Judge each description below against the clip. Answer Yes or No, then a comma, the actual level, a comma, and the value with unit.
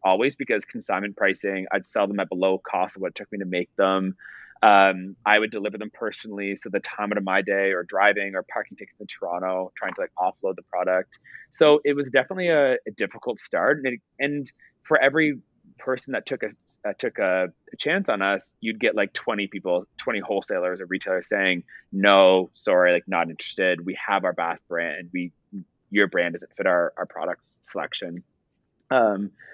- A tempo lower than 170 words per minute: No, average, 195 wpm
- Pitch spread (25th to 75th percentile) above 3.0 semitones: No, narrow, 2.4 semitones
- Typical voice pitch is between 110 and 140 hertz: No, very low, 95 Hz